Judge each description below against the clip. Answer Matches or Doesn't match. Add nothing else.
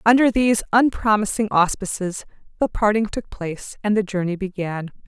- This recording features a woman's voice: Matches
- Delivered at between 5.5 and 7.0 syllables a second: Doesn't match